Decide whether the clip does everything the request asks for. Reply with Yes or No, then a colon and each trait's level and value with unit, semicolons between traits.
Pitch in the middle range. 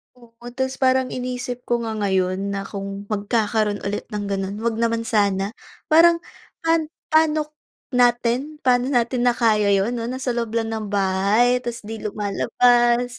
No: high, 235 Hz